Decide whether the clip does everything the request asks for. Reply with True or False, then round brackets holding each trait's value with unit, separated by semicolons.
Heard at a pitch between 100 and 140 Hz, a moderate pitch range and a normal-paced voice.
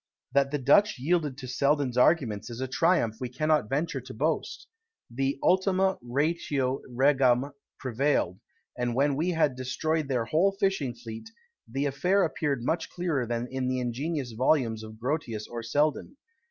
True (135 Hz; 4.2 semitones; 155 wpm)